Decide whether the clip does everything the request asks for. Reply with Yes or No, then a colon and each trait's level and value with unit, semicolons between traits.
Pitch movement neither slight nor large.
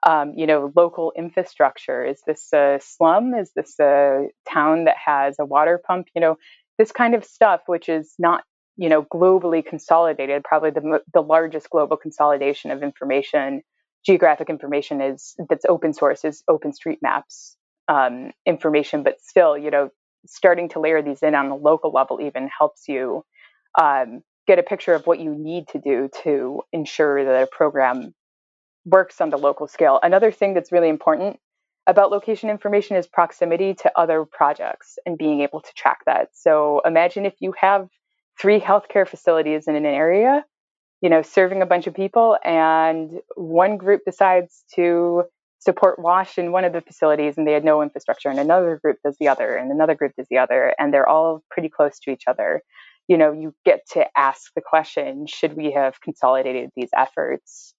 Yes: average, 3.5 semitones